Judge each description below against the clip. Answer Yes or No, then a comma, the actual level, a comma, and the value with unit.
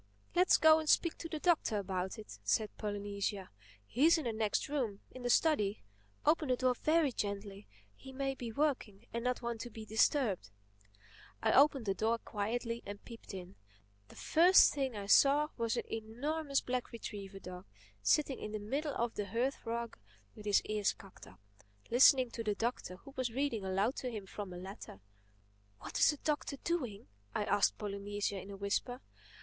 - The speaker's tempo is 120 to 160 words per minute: No, average, 180 wpm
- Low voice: No, high, 230 Hz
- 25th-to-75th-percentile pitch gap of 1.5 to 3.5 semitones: No, average, 5.0 semitones